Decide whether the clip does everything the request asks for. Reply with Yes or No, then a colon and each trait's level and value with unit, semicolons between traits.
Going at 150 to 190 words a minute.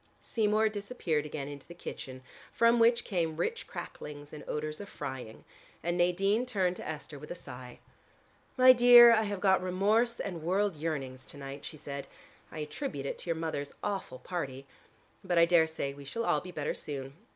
Yes: average, 185 wpm